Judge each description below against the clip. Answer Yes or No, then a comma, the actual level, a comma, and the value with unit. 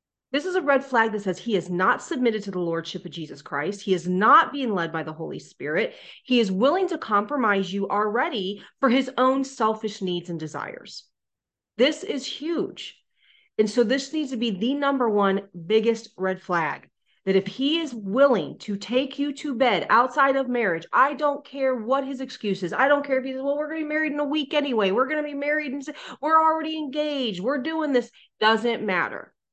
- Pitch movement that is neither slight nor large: No, wide, 6.0 semitones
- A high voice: Yes, very high, 250 Hz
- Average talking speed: No, fast, 215 wpm